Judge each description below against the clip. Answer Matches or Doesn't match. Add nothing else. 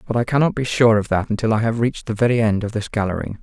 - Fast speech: Matches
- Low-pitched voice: Matches